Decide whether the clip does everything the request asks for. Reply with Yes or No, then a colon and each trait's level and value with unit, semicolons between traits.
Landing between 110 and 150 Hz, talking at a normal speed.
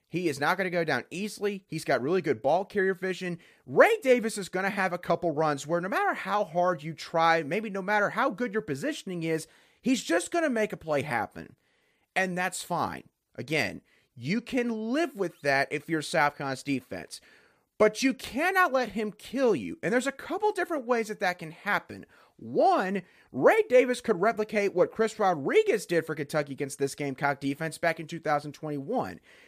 No: medium, 185 Hz; average, 195 wpm